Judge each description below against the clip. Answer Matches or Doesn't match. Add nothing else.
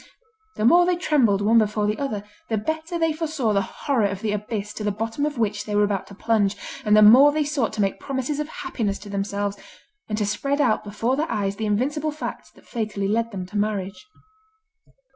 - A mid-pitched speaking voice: Doesn't match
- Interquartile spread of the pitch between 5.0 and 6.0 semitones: Matches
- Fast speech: Matches